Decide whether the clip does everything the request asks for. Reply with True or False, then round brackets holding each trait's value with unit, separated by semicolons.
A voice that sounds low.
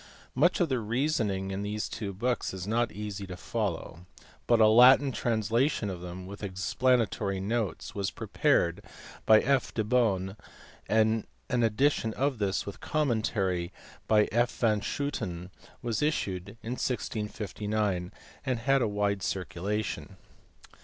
True (105 Hz)